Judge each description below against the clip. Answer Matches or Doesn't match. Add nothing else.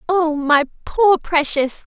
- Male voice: Doesn't match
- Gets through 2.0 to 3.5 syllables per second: Matches